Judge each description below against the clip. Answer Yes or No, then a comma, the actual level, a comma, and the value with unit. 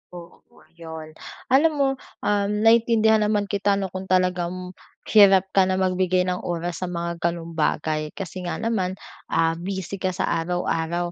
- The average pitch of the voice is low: No, medium, 185 Hz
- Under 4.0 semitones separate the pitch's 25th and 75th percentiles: Yes, narrow, 2.6 semitones